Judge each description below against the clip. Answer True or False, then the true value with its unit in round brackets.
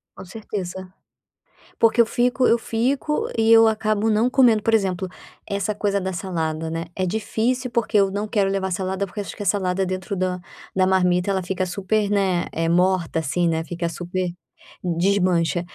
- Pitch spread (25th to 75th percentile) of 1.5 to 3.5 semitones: True (3.2 semitones)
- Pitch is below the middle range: False (190 Hz)